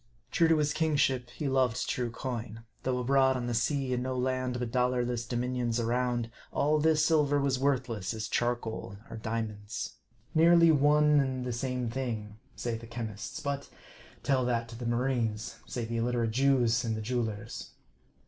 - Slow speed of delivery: No, average, 165 wpm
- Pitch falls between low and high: No, low, 125 Hz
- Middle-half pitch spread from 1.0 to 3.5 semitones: Yes, narrow, 2.6 semitones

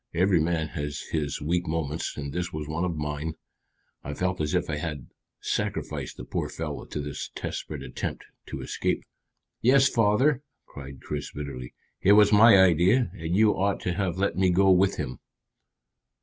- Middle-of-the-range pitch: No, very low, 85 Hz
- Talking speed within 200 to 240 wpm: No, average, 175 wpm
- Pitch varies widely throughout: No, average, 4.7 semitones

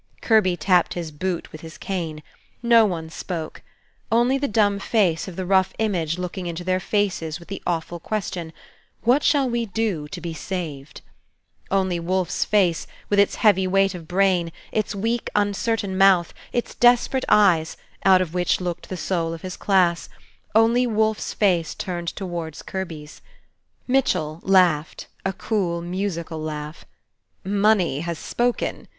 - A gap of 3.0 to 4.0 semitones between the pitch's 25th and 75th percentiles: Yes, average, 3.4 semitones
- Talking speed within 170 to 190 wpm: No, average, 150 wpm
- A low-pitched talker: No, medium, 185 Hz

